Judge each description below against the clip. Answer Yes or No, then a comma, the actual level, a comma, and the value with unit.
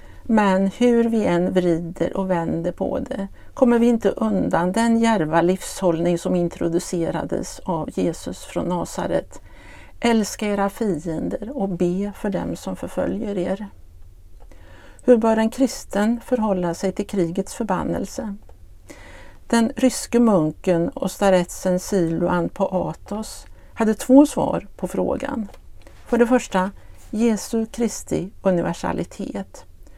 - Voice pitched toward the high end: Yes, high, 195 Hz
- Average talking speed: No, slow, 120 wpm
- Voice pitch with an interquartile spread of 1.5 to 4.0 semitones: No, average, 4.5 semitones